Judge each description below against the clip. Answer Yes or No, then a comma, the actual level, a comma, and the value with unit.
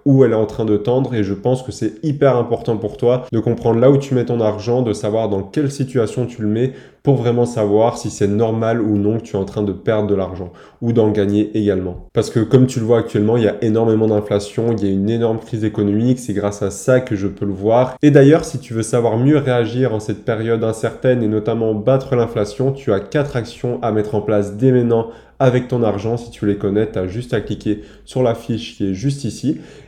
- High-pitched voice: No, low, 115 Hz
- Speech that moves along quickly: Yes, fast, 255 wpm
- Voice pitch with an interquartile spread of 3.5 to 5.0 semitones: No, average, 2.9 semitones